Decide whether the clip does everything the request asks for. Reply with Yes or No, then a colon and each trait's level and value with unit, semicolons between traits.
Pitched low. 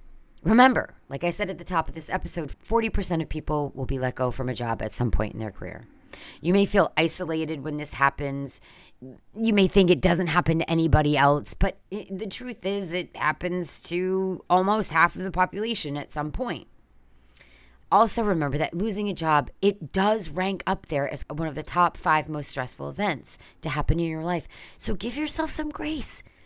No: medium, 165 Hz